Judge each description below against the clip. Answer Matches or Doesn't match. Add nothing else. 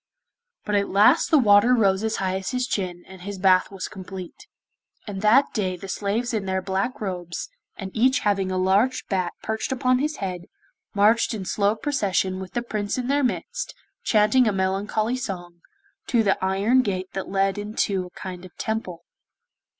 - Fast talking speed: Doesn't match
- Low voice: Doesn't match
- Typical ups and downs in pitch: Matches